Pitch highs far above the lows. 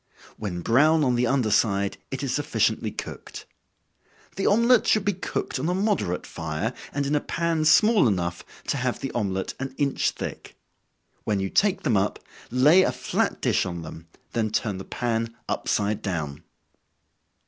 Yes: wide, 8.0 semitones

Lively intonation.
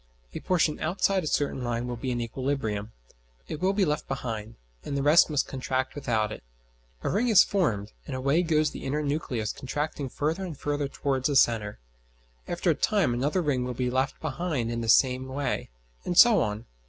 No: average, 4.4 semitones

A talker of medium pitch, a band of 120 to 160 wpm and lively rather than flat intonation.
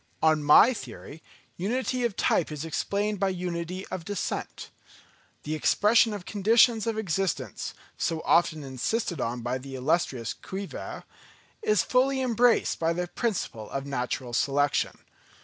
Yes: medium, 175 Hz; slow, 135 wpm; wide, 7.2 semitones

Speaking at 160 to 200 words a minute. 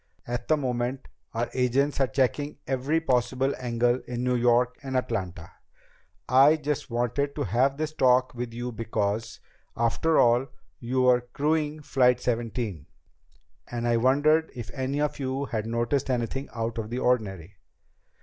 No: average, 150 wpm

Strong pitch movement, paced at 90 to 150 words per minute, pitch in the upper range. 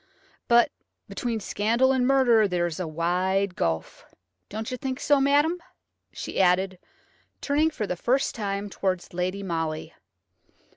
Yes: wide, 6.2 semitones; average, 140 wpm; high, 200 Hz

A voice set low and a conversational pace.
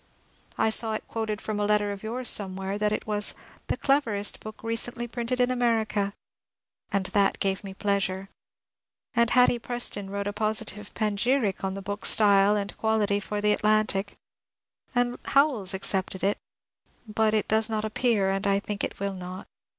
No: high, 210 Hz; average, 175 wpm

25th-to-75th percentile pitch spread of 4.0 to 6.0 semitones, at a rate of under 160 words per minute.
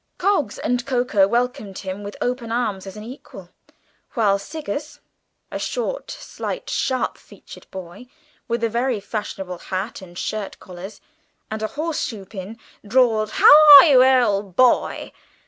Yes: average, 4.4 semitones; average, 145 wpm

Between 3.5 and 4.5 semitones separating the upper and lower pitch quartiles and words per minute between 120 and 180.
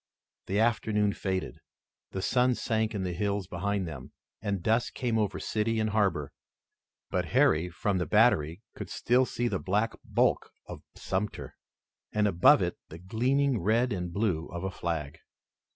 Yes: average, 3.8 semitones; average, 160 wpm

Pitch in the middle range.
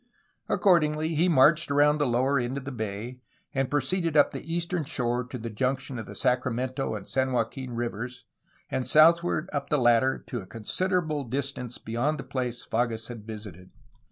No: low, 130 Hz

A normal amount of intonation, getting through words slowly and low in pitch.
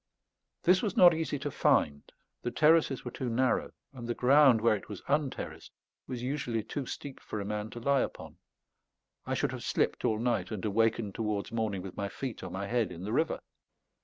No: average, 4.5 semitones; average, 200 wpm; low, 120 Hz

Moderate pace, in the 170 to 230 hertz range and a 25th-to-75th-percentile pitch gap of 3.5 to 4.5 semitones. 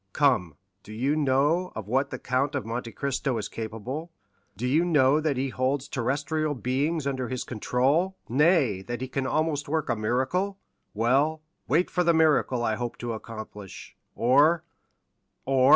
No: average, 160 wpm; low, 135 Hz; average, 4.2 semitones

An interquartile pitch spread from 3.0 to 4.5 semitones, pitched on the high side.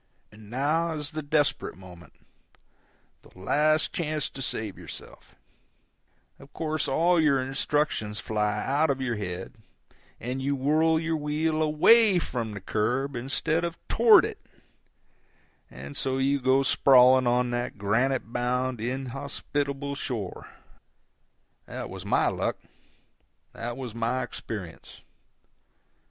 No: average, 4.2 semitones; low, 135 Hz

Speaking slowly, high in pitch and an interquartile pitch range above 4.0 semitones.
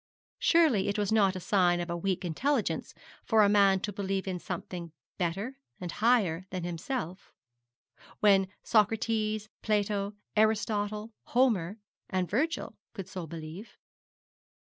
No: slow, 130 wpm; high, 200 Hz; average, 3.1 semitones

